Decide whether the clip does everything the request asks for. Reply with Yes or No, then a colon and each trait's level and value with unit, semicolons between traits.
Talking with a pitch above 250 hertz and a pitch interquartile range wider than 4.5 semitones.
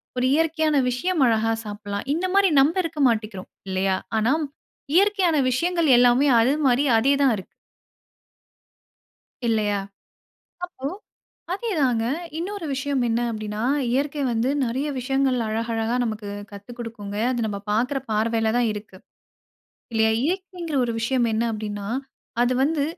No: high, 245 Hz; average, 5.0 semitones